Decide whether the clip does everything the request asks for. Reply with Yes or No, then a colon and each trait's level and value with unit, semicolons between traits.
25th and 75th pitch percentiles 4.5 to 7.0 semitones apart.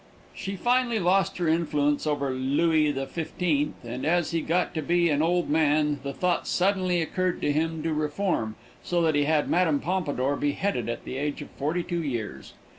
No: average, 3.4 semitones